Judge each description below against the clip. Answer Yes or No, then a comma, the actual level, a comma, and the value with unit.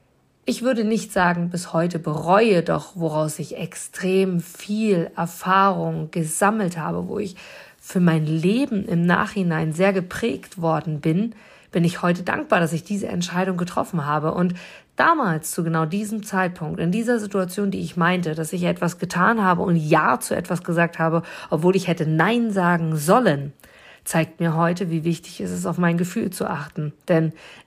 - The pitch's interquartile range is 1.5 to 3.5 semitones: Yes, average, 3.0 semitones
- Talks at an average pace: Yes, average, 170 wpm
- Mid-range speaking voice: Yes, medium, 175 Hz